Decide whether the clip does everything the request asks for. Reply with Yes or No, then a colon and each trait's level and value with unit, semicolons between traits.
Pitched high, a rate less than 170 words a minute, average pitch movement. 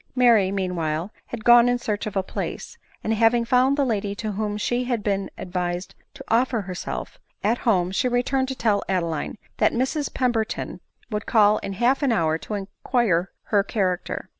No: high, 215 Hz; average, 180 wpm; average, 4.1 semitones